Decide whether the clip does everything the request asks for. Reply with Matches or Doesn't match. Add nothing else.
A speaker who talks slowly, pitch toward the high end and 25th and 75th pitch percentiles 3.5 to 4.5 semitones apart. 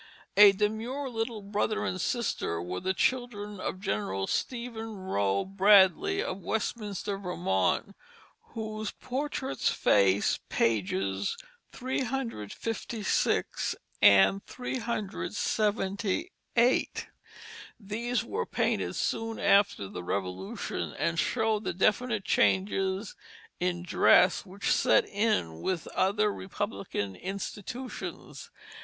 Matches